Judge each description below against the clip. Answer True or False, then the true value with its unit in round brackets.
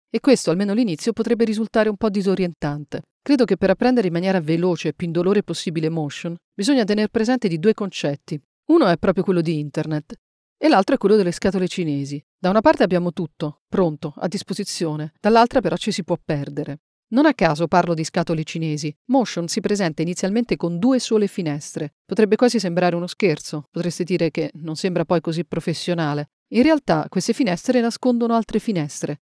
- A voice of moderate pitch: True (180 Hz)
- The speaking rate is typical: False (180 wpm)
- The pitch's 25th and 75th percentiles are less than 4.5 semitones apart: False (5.1 semitones)